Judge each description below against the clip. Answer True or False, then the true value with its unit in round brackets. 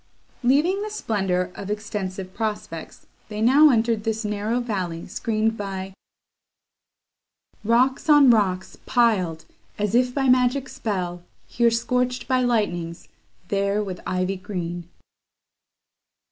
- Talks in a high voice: True (215 Hz)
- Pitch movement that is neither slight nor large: True (4.7 semitones)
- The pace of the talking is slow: True (115 wpm)